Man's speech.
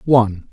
Yes: male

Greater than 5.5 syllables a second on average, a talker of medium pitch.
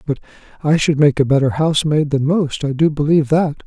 Yes: 6.0 syllables/s; medium, 150 Hz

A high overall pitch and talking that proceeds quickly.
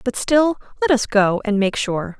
Yes: high, 230 Hz; fast, 220 wpm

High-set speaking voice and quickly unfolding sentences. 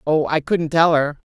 No: medium, 155 Hz; fast, 230 wpm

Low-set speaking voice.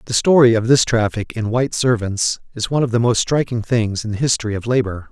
Yes: low, 115 Hz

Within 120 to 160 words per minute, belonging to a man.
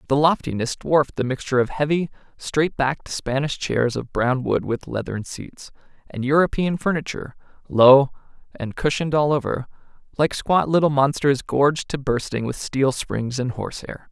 Yes: average, 155 wpm; male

